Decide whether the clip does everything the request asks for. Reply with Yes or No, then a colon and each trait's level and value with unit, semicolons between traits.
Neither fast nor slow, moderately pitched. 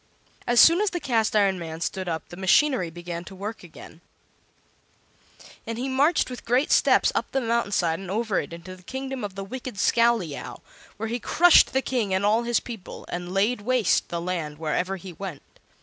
No: average, 195 wpm; high, 205 Hz